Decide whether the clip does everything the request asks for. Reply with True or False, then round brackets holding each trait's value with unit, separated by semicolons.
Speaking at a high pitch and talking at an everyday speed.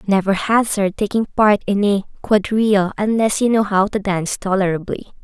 True (205 Hz; 160 wpm)